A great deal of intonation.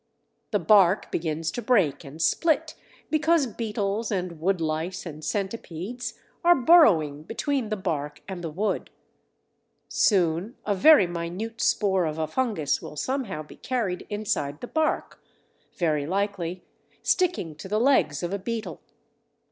Yes: wide, 6.1 semitones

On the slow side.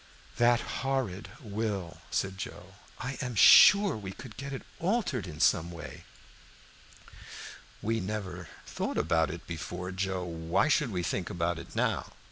No: average, 145 wpm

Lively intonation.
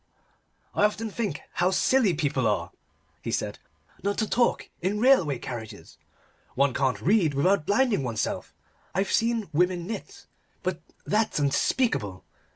Yes: wide, 7.8 semitones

